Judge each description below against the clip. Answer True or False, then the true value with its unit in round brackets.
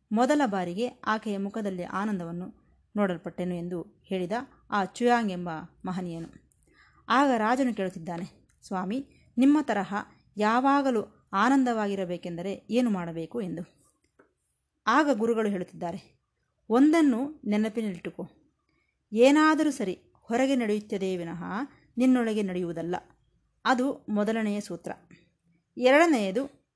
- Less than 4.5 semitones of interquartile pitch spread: False (5.6 semitones)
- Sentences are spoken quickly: False (85 wpm)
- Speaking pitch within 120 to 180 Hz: False (210 Hz)